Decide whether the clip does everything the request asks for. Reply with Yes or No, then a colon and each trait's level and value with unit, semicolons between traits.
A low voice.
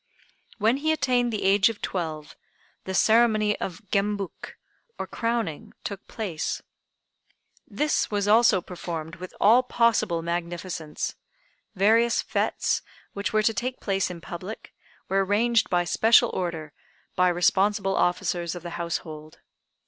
No: high, 195 Hz